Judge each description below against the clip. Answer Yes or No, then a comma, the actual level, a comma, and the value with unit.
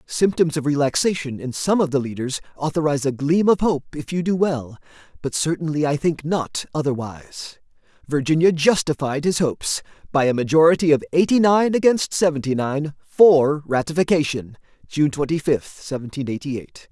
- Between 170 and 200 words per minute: No, average, 155 wpm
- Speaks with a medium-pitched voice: Yes, medium, 150 Hz